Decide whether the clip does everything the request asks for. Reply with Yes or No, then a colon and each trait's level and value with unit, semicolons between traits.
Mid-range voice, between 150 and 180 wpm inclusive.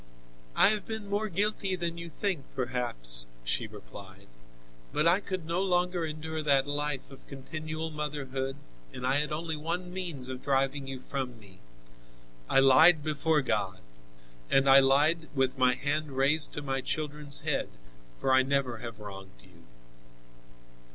Yes: medium, 145 Hz; average, 155 wpm